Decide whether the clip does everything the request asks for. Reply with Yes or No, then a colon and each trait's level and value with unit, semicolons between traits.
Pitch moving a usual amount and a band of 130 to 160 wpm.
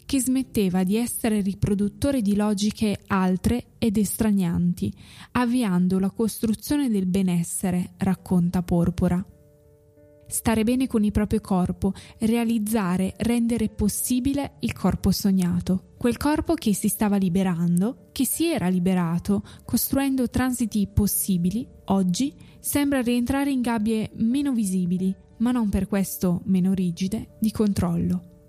No: average, 4.1 semitones; average, 120 wpm